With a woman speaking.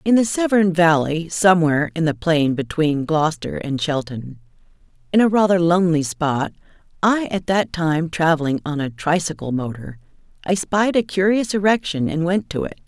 Yes: female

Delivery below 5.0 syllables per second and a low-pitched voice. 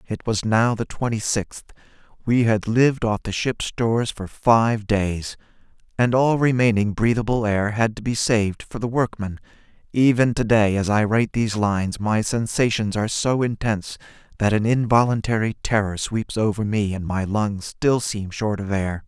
Yes: 4.8 syllables/s; low, 110 Hz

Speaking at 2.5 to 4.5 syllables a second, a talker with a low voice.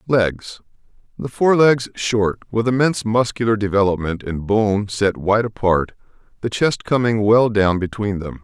Yes: 4.4 syllables/s; low, 110 Hz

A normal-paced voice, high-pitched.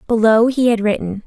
Yes: average, 190 wpm; high, 220 Hz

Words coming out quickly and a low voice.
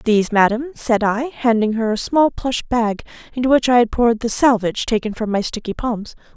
No: fast, 210 wpm; high, 230 Hz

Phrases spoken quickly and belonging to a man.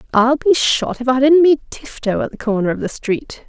No: fast, 240 wpm; female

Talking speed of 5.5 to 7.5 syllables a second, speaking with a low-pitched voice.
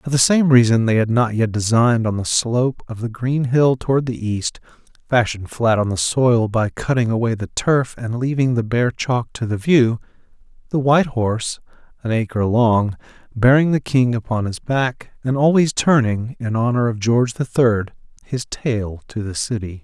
No: 4.8 syllables/s; low, 120 Hz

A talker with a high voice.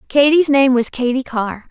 Yes: very high, 260 Hz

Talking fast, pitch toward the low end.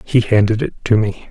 Yes: fast, 230 wpm; low, 110 Hz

